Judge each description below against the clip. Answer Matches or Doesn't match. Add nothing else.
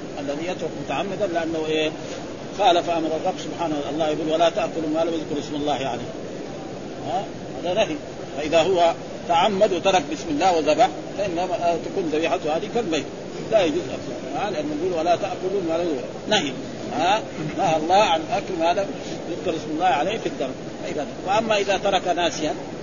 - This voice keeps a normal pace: Doesn't match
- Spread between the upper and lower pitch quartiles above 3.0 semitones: Doesn't match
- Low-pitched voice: Doesn't match